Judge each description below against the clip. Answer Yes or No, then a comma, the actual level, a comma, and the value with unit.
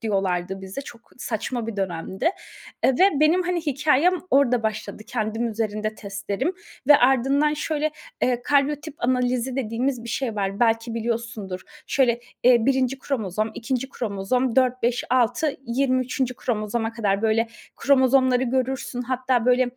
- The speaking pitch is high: Yes, high, 245 Hz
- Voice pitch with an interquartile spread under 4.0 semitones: Yes, average, 3.2 semitones